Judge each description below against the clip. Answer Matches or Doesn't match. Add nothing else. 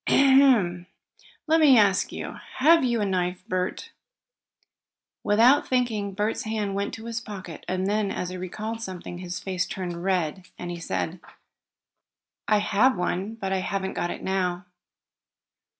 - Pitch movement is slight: Doesn't match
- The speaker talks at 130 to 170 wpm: Matches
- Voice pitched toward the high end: Matches